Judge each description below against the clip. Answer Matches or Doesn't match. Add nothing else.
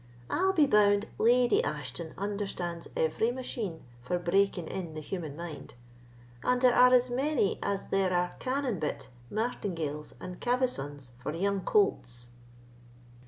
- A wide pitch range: Matches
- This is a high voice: Matches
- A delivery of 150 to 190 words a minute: Doesn't match